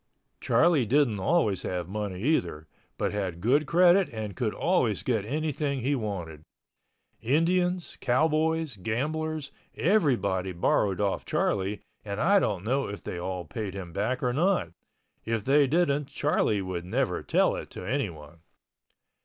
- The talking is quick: No, average, 140 wpm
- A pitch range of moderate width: No, wide, 7.8 semitones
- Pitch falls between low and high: No, low, 120 Hz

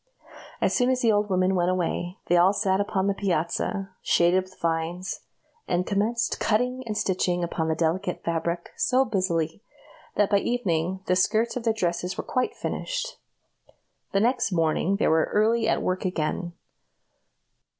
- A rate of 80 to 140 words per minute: No, average, 160 wpm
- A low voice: No, high, 190 Hz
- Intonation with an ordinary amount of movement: Yes, average, 3.8 semitones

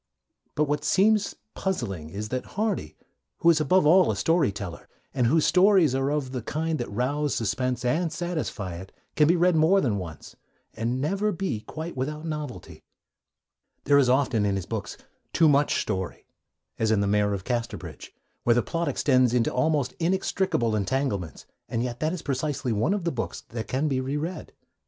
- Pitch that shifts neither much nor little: No, wide, 6.0 semitones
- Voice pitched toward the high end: No, medium, 140 Hz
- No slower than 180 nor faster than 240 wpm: Yes, average, 185 wpm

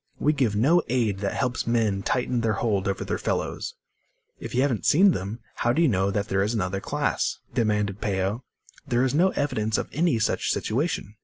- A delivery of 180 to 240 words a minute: Yes, average, 190 wpm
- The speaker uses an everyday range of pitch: Yes, average, 4.2 semitones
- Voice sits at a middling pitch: No, low, 115 Hz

